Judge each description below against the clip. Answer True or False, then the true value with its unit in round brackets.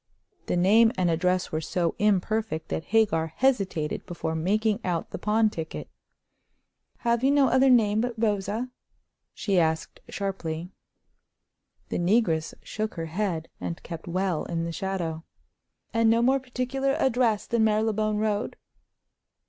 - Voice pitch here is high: True (205 Hz)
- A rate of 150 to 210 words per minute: False (140 wpm)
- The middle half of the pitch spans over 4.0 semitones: True (5.0 semitones)